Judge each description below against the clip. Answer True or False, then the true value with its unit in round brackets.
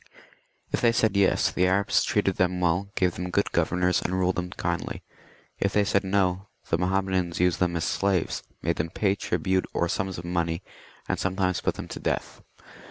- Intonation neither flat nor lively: False (1.6 semitones)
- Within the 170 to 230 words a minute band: True (190 wpm)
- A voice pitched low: True (90 Hz)